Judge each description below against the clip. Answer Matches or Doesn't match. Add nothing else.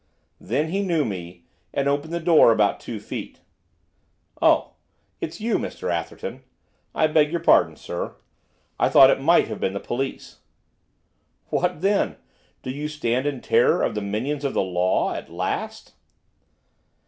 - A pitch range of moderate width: Doesn't match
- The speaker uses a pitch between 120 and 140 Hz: Matches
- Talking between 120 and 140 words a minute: Doesn't match